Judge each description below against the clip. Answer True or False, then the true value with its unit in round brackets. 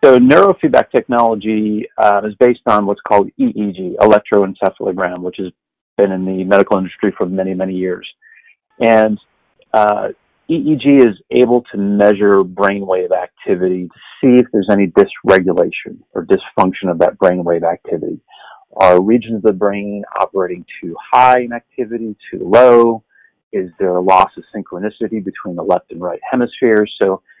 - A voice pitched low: True (105 Hz)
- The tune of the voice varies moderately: True (3.3 semitones)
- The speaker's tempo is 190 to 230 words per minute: False (150 wpm)